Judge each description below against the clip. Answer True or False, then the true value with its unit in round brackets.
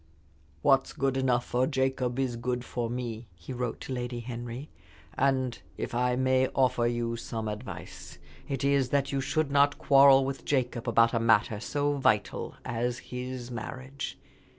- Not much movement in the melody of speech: True (2.2 semitones)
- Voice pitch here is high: False (125 Hz)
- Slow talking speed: False (160 wpm)